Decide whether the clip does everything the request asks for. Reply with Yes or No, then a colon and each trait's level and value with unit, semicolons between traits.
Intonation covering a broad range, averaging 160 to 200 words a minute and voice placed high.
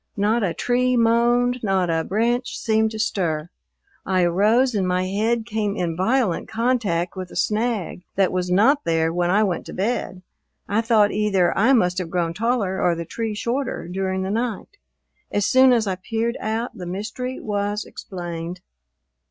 No: average, 4.2 semitones; average, 175 wpm; high, 205 Hz